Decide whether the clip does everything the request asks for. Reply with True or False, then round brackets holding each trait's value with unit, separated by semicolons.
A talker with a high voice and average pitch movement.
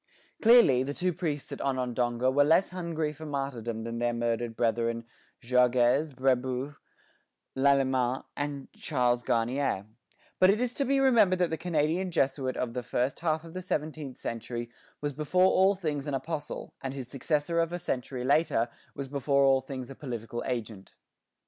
False (135 Hz; 4.3 semitones)